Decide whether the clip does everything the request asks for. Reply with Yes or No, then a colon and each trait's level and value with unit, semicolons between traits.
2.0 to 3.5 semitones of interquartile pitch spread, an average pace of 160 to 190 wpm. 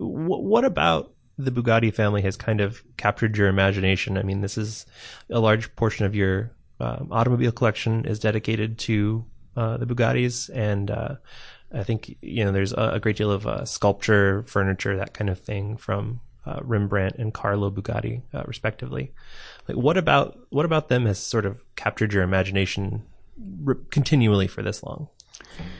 Yes: average, 2.8 semitones; average, 165 wpm